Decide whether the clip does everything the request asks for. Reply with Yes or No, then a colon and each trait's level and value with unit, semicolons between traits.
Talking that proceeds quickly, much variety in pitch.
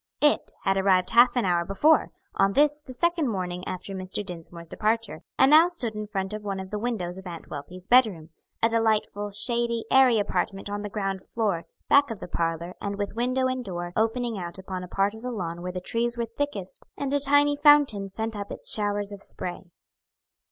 No: fast, 210 wpm; average, 4.4 semitones